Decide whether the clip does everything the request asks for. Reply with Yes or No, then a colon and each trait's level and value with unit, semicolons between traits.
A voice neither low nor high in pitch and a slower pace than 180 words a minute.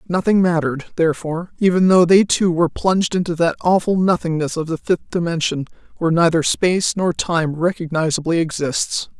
Yes: medium, 170 Hz; average, 155 wpm